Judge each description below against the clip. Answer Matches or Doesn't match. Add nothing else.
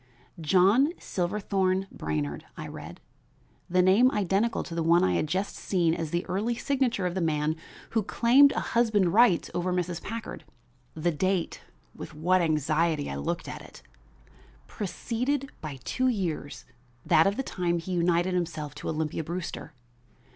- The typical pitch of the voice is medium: Matches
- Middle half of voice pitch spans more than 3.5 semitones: Matches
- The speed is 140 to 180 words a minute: Matches